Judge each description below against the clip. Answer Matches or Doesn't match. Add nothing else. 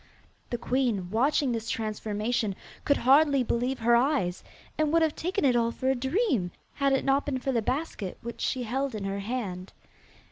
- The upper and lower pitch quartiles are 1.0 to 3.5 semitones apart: Doesn't match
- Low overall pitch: Doesn't match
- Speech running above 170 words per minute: Matches